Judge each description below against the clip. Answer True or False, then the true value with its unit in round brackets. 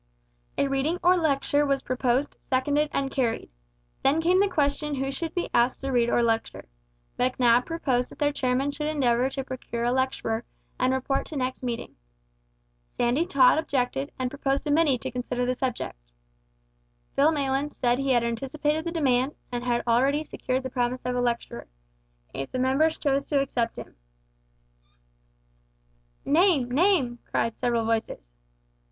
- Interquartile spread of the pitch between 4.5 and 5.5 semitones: False (3.0 semitones)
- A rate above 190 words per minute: False (160 wpm)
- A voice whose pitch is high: True (265 Hz)